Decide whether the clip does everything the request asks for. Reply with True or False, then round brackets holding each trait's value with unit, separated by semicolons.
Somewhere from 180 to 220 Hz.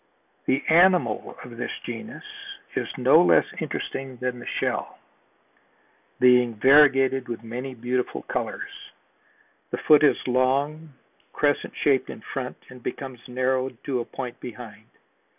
False (130 Hz)